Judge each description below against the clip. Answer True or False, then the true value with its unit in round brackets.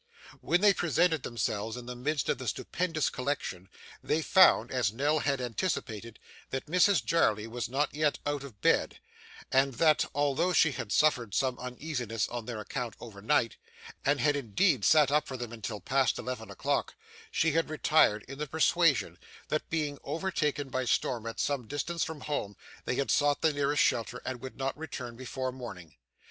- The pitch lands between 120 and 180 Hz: True (135 Hz)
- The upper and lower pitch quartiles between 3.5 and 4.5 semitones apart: True (4.2 semitones)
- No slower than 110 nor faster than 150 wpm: False (175 wpm)